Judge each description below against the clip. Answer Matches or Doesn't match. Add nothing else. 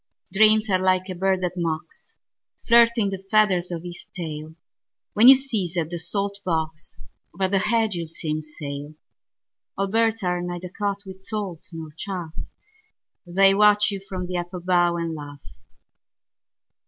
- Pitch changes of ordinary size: Matches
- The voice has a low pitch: Doesn't match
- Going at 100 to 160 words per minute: Matches